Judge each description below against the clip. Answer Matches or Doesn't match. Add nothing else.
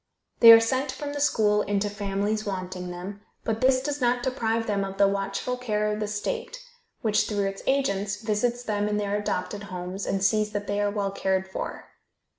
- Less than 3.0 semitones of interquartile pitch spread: Matches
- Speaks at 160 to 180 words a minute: Doesn't match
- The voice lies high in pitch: Matches